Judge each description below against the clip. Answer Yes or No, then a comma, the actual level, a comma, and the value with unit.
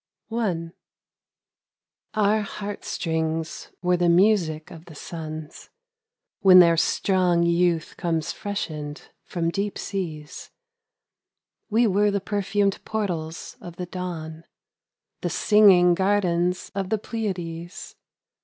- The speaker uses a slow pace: Yes, slow, 115 wpm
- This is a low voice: No, medium, 180 Hz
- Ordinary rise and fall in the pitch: Yes, average, 3.4 semitones